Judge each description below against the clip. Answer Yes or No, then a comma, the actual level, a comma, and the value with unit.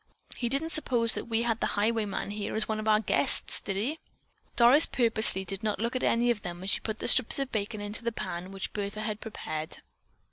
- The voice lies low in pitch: No, high, 220 Hz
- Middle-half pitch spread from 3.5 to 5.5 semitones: No, narrow, 2.6 semitones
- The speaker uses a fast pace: Yes, fast, 225 wpm